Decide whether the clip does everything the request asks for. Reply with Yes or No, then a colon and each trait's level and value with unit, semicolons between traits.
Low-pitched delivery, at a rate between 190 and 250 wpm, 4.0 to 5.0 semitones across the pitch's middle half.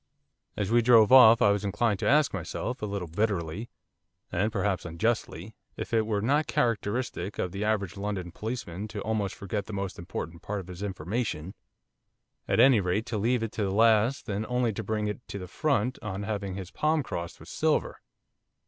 No: low, 105 Hz; average, 195 wpm; average, 2.9 semitones